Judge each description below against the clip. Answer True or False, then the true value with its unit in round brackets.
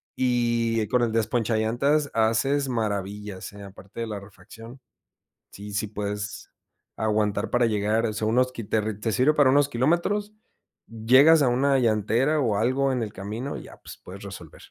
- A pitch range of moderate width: True (3.7 semitones)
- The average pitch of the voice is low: True (115 Hz)